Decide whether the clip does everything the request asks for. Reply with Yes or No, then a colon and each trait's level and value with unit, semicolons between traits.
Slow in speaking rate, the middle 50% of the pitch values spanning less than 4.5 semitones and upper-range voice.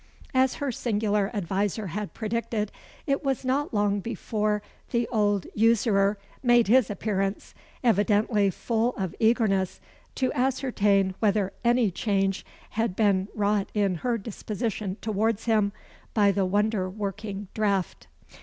Yes: slow, 125 wpm; narrow, 2.6 semitones; high, 210 Hz